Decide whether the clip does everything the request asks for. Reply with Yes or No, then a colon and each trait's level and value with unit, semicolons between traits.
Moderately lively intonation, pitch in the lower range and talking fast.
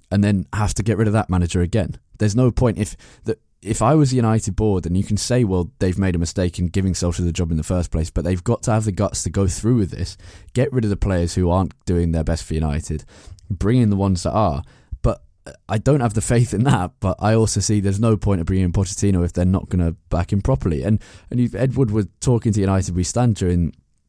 Yes: average, 3.8 semitones; low, 100 Hz; fast, 265 wpm